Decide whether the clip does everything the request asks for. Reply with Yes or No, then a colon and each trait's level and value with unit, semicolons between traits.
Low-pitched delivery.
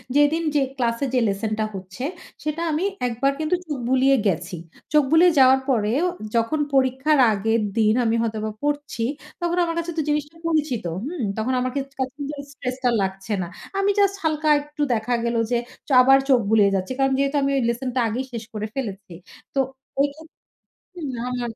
No: very high, 260 Hz